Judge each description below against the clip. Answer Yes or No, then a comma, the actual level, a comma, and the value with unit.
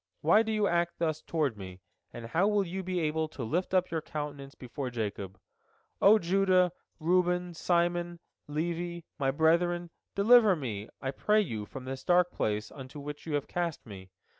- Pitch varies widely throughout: No, average, 4.8 semitones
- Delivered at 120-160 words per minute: No, average, 175 wpm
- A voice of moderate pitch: Yes, medium, 165 Hz